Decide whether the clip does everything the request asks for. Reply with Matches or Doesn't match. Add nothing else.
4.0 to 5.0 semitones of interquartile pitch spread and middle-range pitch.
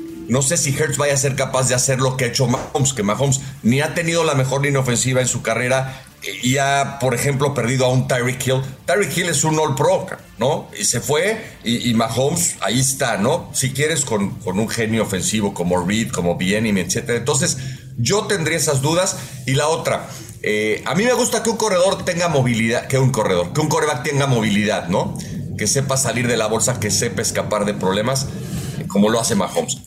Doesn't match